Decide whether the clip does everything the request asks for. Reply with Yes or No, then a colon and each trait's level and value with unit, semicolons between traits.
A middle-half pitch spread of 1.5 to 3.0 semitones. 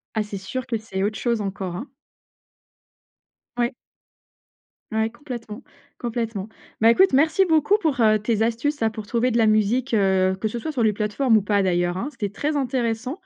No: average, 3.7 semitones